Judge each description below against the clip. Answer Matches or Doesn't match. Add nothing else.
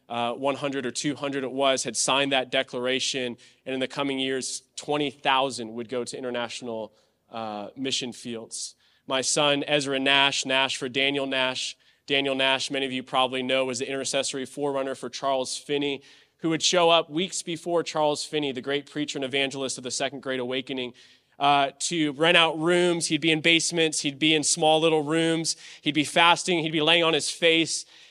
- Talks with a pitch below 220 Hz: Matches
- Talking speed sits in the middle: Matches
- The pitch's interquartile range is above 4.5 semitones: Doesn't match